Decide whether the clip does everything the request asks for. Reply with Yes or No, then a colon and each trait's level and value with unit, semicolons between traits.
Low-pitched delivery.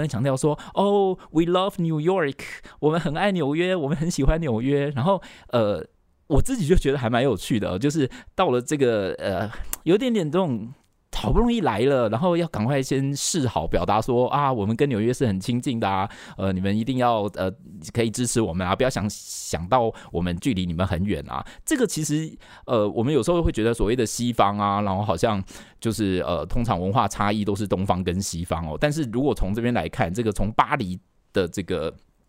Yes: low, 120 Hz